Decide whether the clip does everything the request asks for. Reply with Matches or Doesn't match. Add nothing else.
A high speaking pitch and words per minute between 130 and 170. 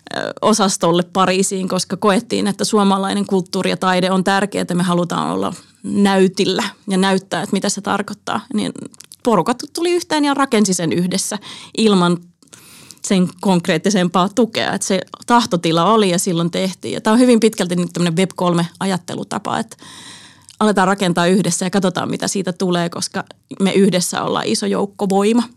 Matches